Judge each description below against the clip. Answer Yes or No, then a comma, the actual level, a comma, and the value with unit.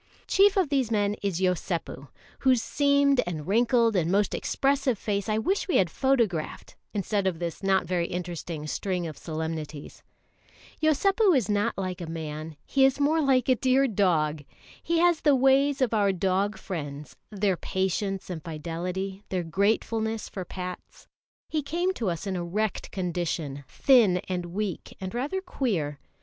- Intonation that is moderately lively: No, wide, 6.9 semitones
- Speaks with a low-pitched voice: No, high, 195 Hz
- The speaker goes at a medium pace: Yes, average, 160 wpm